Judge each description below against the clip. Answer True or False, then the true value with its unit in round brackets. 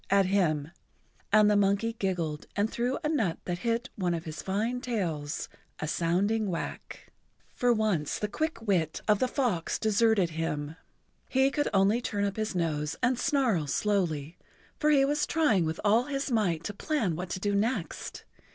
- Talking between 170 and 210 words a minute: True (180 wpm)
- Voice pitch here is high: True (205 Hz)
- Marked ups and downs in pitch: True (5.7 semitones)